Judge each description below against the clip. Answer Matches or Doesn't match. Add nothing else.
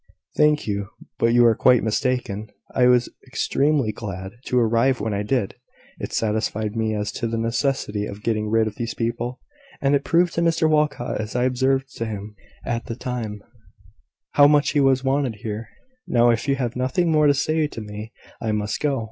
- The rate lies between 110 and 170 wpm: Doesn't match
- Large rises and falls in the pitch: Doesn't match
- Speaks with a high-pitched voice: Doesn't match